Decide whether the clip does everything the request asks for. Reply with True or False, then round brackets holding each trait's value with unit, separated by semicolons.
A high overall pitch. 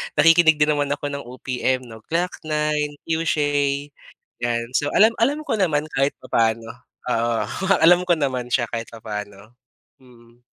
False (140 Hz)